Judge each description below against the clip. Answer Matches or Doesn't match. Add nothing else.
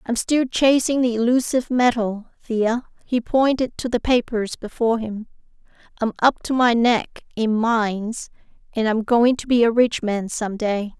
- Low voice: Doesn't match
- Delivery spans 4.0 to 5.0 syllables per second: Matches